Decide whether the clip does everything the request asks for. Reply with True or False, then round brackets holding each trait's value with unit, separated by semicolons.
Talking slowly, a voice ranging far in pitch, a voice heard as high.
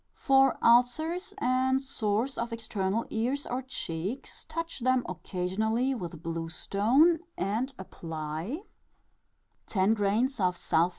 True (105 wpm; 5.9 semitones; 230 Hz)